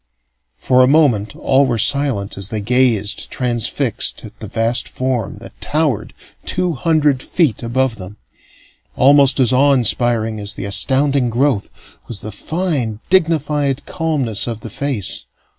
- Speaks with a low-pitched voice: Yes, low, 125 Hz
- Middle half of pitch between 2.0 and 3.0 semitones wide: No, average, 4.4 semitones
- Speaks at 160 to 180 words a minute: No, average, 140 wpm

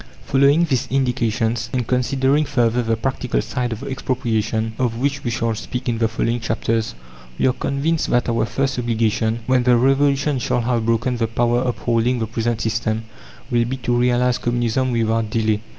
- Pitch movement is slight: Yes, narrow, 2.3 semitones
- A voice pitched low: Yes, low, 120 Hz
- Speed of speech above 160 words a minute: Yes, average, 175 wpm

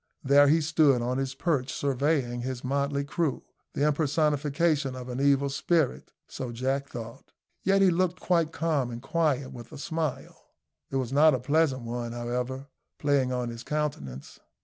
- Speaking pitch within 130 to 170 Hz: Yes, medium, 140 Hz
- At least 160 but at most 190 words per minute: Yes, average, 165 wpm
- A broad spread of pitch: No, average, 3.3 semitones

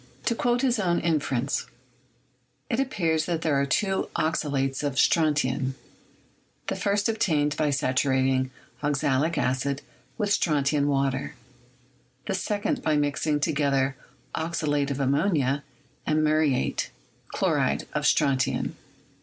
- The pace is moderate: No, slow, 115 wpm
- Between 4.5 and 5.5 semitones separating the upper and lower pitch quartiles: No, average, 3.2 semitones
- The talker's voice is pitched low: No, medium, 145 Hz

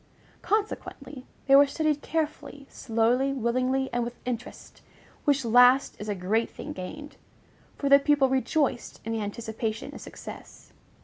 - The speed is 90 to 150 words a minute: Yes, average, 140 wpm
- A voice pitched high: Yes, very high, 260 Hz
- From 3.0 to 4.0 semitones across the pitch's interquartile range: Yes, average, 3.5 semitones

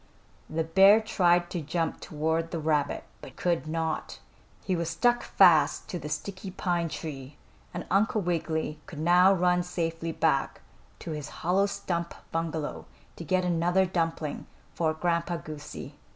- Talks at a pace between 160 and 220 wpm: No, average, 150 wpm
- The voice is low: No, medium, 170 Hz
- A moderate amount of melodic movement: No, narrow, 2.0 semitones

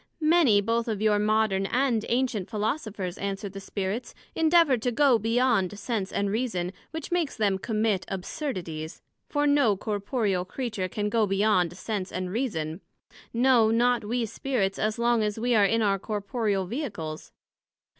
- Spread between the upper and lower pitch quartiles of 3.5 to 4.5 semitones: Yes, average, 3.8 semitones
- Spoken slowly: No, average, 155 wpm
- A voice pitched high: Yes, high, 215 Hz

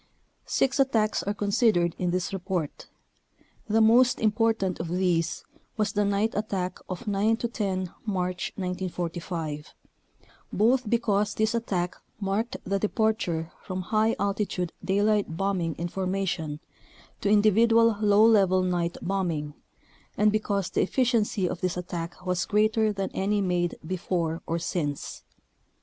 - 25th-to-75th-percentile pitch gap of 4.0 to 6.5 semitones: No, average, 3.3 semitones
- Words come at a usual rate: No, slow, 130 wpm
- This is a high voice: Yes, high, 195 Hz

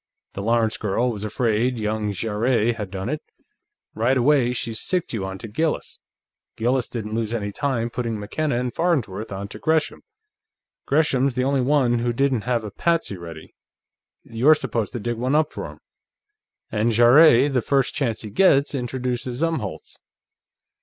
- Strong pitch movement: No, average, 3.7 semitones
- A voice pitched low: Yes, low, 120 Hz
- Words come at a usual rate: Yes, average, 160 wpm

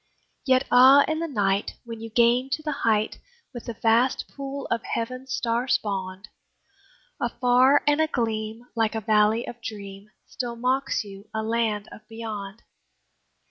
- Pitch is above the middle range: Yes, high, 230 Hz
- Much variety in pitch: No, average, 3.0 semitones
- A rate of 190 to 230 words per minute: No, average, 150 wpm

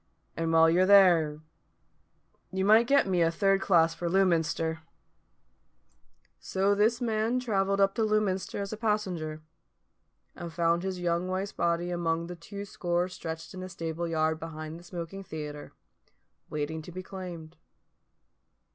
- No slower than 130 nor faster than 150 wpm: Yes, average, 145 wpm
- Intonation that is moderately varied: Yes, average, 3.0 semitones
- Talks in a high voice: No, medium, 175 Hz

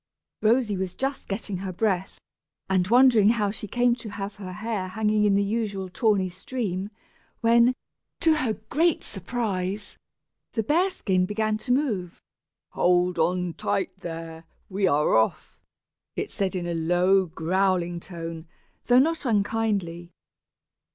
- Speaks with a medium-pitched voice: No, high, 195 Hz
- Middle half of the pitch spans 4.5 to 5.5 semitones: No, average, 3.9 semitones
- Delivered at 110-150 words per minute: Yes, average, 140 wpm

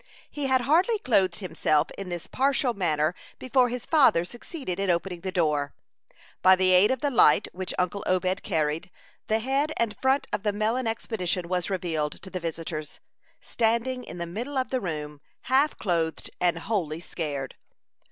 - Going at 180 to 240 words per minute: No, average, 170 wpm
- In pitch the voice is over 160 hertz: Yes, high, 190 Hz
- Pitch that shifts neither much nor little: No, wide, 6.5 semitones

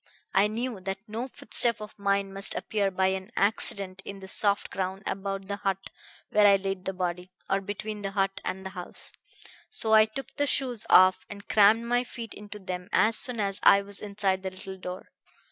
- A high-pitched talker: Yes, high, 200 Hz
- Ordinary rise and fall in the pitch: No, narrow, 2.0 semitones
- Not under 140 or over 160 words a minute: No, average, 200 wpm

